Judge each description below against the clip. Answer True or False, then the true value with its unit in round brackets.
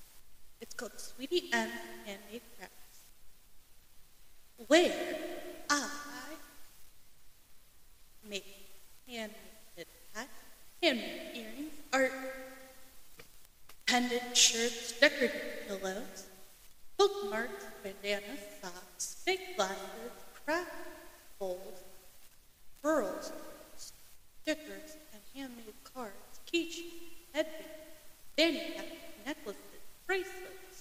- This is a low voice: False (285 Hz)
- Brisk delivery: False (65 wpm)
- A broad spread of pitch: True (6.6 semitones)